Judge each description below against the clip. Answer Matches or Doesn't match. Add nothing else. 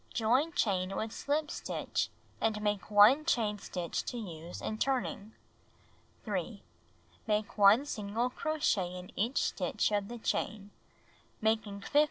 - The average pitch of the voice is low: Doesn't match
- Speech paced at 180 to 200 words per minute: Doesn't match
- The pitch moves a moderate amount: Matches